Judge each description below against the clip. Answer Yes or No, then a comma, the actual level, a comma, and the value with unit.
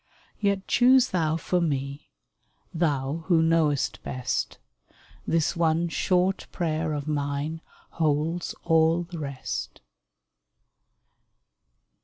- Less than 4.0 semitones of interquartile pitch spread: Yes, average, 2.8 semitones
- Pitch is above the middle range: No, medium, 160 Hz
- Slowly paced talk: Yes, slow, 100 wpm